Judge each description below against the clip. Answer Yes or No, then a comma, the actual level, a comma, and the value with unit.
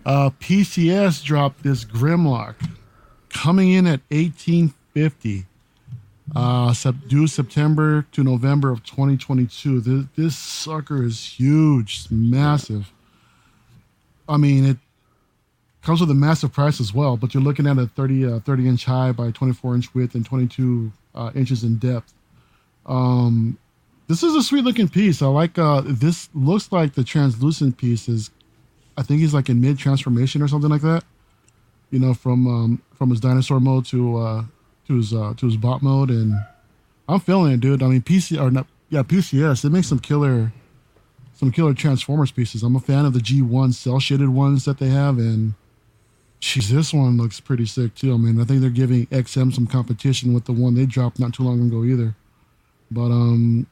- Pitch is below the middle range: Yes, low, 130 Hz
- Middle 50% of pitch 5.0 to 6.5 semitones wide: No, average, 3.2 semitones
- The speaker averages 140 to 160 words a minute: No, average, 175 wpm